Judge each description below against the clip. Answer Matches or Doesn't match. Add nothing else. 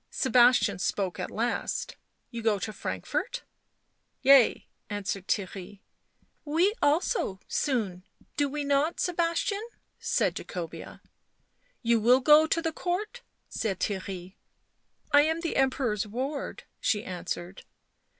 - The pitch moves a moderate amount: Doesn't match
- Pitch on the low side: Doesn't match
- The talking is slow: Matches